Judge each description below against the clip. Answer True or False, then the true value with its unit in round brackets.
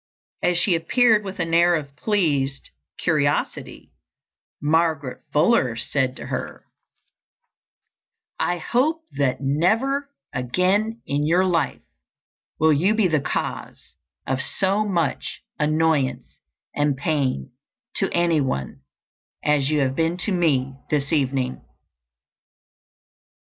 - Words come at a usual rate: False (110 wpm)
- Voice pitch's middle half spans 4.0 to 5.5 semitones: True (4.7 semitones)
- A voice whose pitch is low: False (160 Hz)